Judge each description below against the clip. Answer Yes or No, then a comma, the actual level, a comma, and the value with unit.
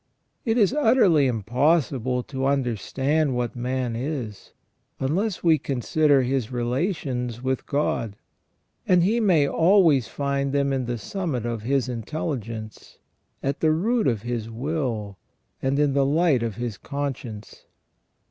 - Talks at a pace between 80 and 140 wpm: Yes, slow, 135 wpm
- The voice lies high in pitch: No, low, 135 Hz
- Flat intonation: No, average, 4.5 semitones